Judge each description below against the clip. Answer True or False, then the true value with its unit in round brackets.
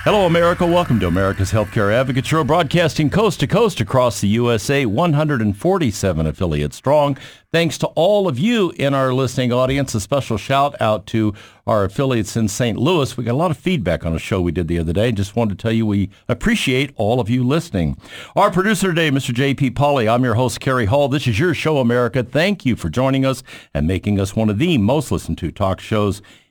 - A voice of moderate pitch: False (125 Hz)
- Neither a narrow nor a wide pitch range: False (5.8 semitones)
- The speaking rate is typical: False (215 wpm)